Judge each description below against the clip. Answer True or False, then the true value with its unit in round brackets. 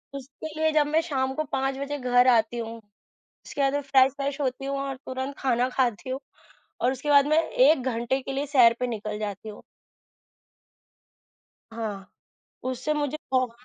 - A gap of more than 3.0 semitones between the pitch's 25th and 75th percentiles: False (2.6 semitones)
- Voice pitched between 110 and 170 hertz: False (265 Hz)